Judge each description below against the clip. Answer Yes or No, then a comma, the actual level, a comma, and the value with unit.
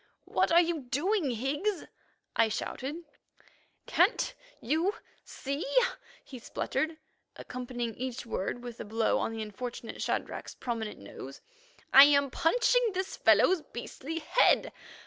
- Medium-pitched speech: No, very high, 270 Hz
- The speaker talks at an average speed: No, slow, 115 wpm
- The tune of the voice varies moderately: No, wide, 6.1 semitones